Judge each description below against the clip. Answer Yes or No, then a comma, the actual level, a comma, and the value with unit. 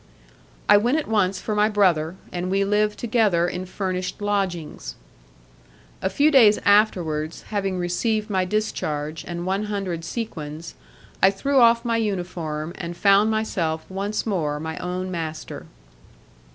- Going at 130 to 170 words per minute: Yes, average, 140 wpm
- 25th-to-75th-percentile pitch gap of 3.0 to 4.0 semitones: Yes, average, 3.7 semitones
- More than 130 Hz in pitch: Yes, high, 190 Hz